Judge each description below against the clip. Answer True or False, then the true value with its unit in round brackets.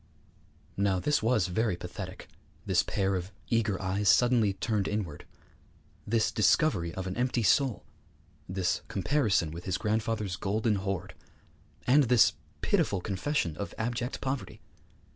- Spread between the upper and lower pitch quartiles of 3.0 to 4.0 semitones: True (3.7 semitones)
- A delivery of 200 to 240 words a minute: False (135 wpm)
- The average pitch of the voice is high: False (105 Hz)